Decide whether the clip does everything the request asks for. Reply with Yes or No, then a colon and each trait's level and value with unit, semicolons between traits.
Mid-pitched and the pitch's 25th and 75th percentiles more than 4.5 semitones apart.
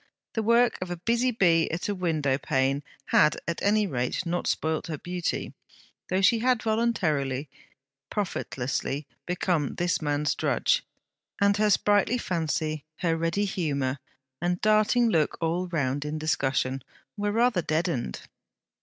Yes: medium, 170 Hz; wide, 5.6 semitones